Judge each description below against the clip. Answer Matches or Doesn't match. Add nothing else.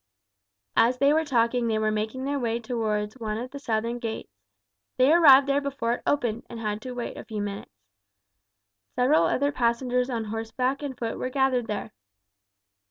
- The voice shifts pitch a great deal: Doesn't match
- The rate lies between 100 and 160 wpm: Doesn't match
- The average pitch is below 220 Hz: Doesn't match